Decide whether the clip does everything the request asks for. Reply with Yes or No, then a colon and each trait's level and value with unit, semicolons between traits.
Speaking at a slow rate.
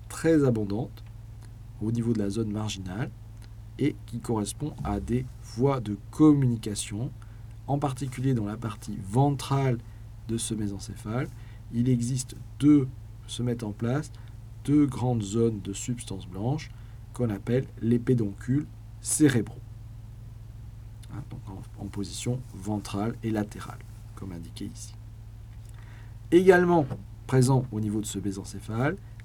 Yes: slow, 125 wpm